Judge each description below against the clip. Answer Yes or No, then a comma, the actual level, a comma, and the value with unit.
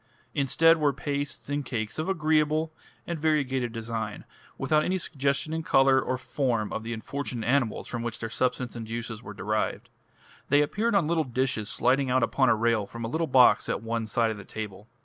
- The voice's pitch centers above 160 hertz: No, low, 130 Hz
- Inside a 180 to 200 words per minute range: Yes, average, 195 wpm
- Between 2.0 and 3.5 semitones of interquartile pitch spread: No, average, 4.7 semitones